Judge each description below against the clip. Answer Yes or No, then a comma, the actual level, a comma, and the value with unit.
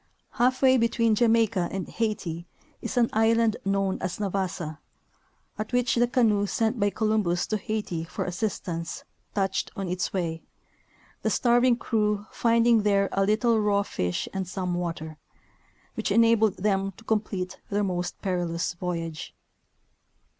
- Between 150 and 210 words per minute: No, average, 140 wpm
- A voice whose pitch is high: Yes, high, 205 Hz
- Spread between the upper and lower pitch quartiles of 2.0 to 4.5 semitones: Yes, average, 3.9 semitones